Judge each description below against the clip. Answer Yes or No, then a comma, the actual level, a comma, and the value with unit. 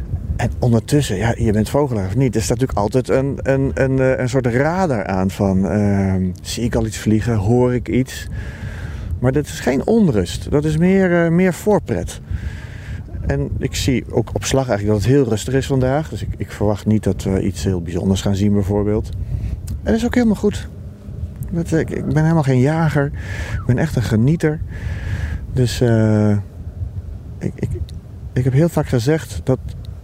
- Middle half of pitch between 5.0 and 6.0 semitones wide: Yes, average, 5.3 semitones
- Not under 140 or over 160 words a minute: No, average, 190 wpm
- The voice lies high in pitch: No, low, 110 Hz